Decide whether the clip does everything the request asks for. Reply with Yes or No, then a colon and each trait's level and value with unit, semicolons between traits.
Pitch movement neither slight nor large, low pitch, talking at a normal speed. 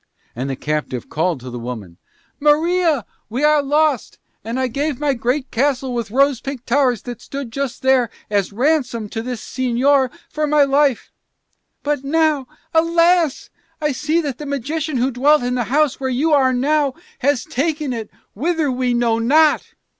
No: average, 3.7 semitones; very high, 270 Hz; average, 170 wpm